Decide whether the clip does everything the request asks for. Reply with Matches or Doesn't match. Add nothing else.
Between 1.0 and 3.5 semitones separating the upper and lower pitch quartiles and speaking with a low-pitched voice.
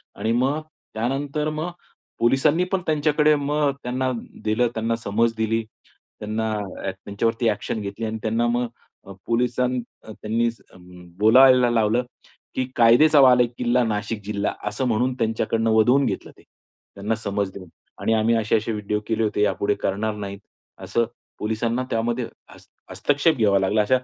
Matches